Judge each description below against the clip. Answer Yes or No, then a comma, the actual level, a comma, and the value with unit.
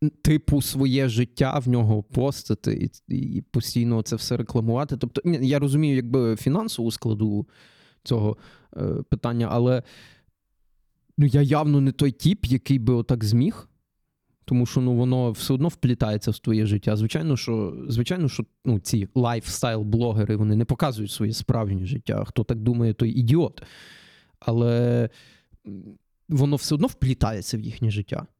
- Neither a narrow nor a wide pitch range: Yes, average, 3.4 semitones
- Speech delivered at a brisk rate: No, average, 145 wpm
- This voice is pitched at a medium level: No, low, 120 Hz